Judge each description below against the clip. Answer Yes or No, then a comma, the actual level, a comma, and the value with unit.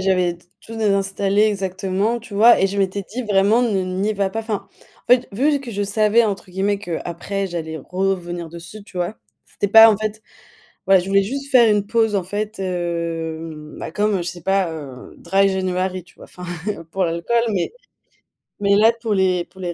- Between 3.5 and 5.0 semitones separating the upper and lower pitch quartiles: No, average, 2.9 semitones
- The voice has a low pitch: No, high, 195 Hz